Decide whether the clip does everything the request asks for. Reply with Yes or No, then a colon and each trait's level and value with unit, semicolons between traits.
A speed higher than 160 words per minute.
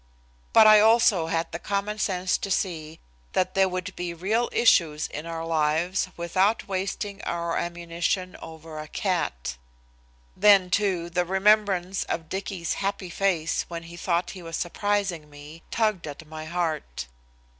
No: average, 150 wpm